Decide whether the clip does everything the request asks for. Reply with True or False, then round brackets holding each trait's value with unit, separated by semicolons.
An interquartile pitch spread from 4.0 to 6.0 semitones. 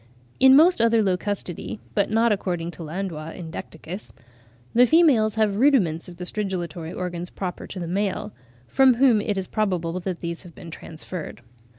True (4.3 semitones)